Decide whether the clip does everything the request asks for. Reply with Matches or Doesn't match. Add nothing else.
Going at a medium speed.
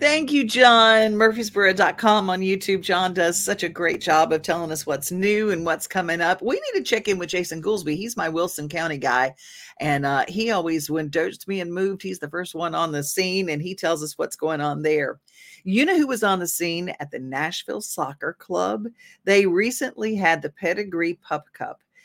Doesn't match